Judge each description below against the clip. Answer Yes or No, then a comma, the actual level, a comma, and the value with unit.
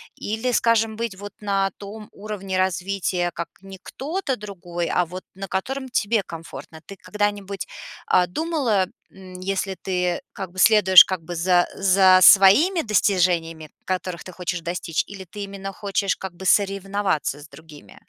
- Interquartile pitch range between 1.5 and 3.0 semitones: Yes, narrow, 2.4 semitones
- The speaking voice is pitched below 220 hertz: Yes, high, 190 Hz